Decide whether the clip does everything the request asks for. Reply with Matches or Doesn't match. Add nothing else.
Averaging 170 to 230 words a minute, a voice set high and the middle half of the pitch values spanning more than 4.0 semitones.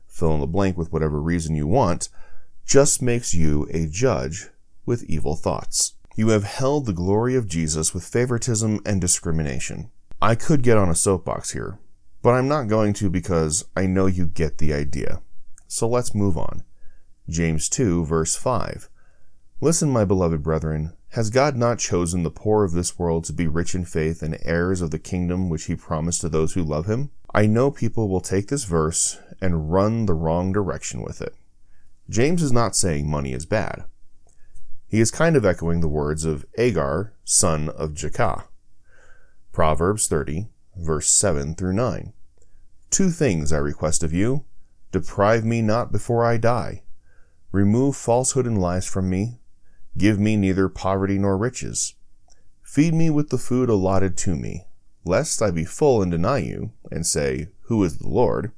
Doesn't match